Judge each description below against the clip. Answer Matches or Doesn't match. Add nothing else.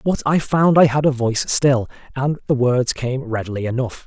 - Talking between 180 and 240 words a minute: Matches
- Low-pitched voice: Matches